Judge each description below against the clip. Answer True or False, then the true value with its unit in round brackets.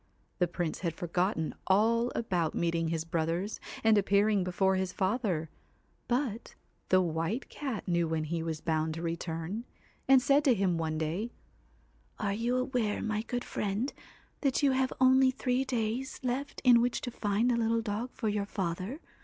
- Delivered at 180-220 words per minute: False (170 wpm)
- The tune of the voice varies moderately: False (6.3 semitones)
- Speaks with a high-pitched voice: True (205 Hz)